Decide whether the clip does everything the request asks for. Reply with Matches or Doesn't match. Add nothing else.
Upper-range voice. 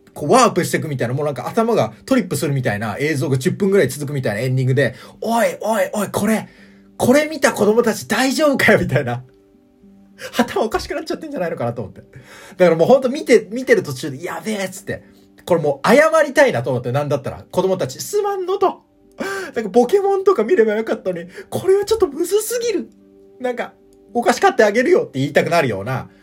Matches